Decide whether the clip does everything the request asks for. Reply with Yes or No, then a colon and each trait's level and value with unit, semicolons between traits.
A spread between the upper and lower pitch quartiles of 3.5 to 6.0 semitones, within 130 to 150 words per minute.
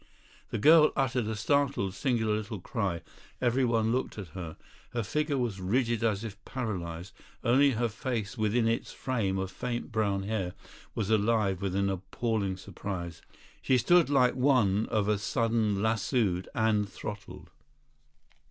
Yes: average, 3.8 semitones; average, 145 wpm